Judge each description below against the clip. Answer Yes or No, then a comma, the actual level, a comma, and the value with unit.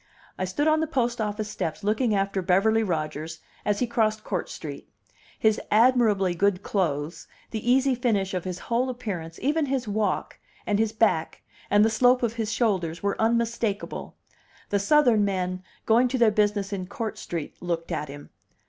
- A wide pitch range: No, average, 4.1 semitones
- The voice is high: Yes, high, 210 Hz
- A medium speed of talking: Yes, average, 175 wpm